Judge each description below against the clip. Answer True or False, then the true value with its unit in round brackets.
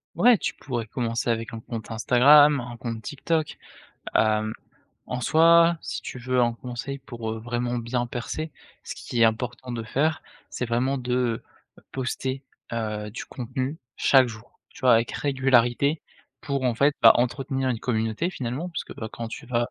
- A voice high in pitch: False (125 Hz)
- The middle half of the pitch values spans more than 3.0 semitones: False (2.7 semitones)